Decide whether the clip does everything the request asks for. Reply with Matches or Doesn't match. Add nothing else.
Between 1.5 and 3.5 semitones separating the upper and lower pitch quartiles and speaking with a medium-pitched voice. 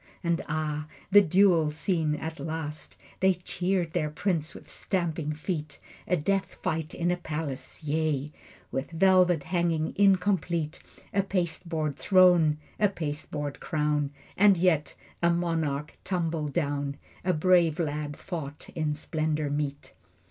Matches